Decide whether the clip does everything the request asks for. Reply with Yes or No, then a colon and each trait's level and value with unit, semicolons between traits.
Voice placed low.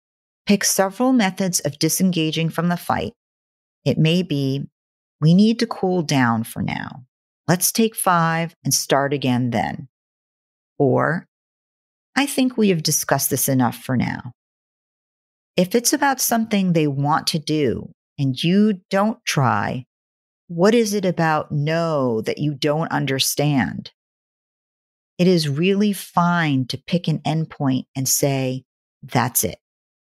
No: medium, 160 Hz